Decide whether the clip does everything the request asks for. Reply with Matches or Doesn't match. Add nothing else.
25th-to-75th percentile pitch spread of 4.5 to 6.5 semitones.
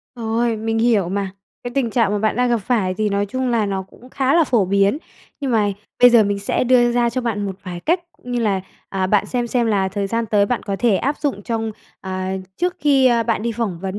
Doesn't match